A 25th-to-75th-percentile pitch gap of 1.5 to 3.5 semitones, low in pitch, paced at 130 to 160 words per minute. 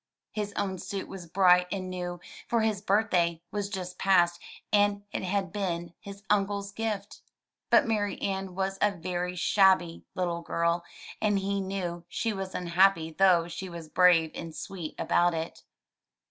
No: narrow, 2.5 semitones; high, 190 Hz; average, 155 wpm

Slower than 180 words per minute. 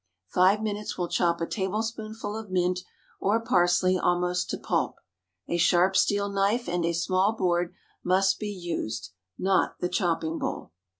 Yes: average, 155 wpm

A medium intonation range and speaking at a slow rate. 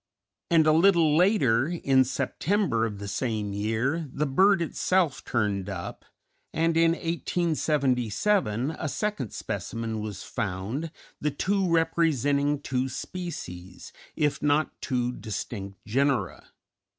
No: wide, 6.7 semitones; slow, 115 wpm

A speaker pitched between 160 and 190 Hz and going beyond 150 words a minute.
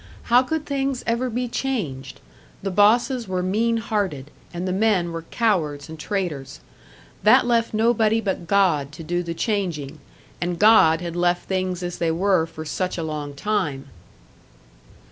Yes: medium, 185 Hz; average, 160 wpm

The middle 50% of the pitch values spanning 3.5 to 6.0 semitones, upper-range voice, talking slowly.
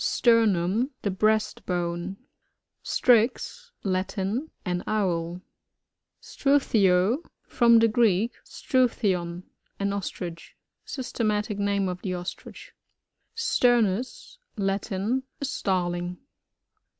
Yes: average, 4.4 semitones; high, 200 Hz; slow, 95 wpm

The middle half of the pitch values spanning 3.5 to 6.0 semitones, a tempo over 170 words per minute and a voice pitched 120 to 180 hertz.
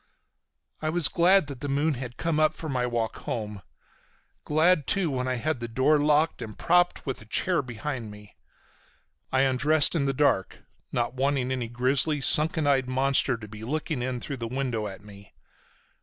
Yes: average, 4.2 semitones; average, 180 wpm; low, 135 Hz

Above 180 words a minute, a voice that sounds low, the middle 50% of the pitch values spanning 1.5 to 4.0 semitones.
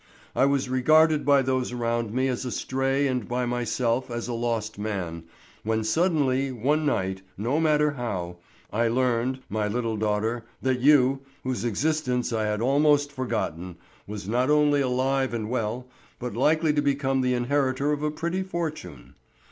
No: average, 165 wpm; low, 125 Hz; average, 3.7 semitones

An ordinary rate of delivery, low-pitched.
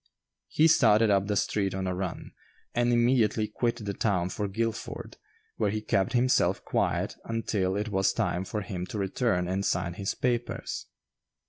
Yes: average, 165 wpm; low, 105 Hz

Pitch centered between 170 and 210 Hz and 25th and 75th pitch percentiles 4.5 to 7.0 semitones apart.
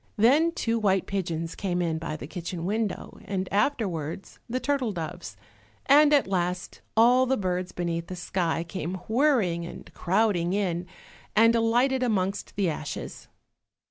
Yes: high, 190 Hz; average, 5.0 semitones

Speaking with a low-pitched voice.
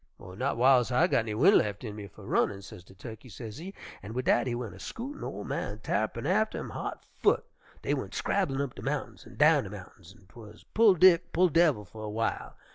Yes: low, 120 Hz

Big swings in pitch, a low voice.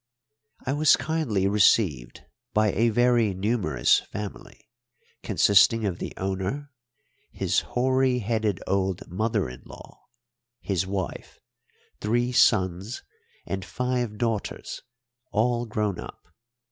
No: average, 4.1 semitones; low, 105 Hz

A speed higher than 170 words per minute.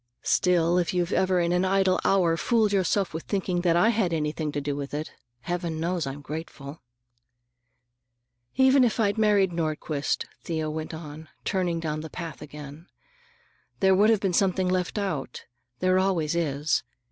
No: average, 160 wpm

